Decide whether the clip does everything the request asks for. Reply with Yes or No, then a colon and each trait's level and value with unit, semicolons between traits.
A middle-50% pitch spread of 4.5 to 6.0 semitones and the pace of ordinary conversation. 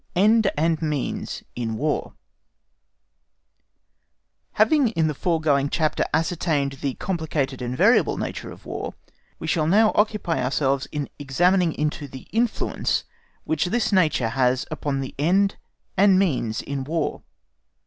No: average, 5.1 semitones; slow, 130 wpm